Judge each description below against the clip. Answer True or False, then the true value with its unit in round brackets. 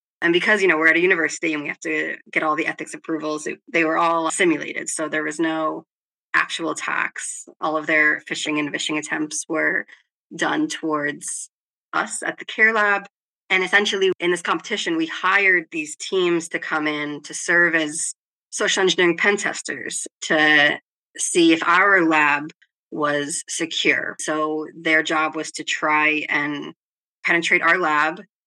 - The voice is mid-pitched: True (160 Hz)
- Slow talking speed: False (165 wpm)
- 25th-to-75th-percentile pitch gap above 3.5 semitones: True (4.0 semitones)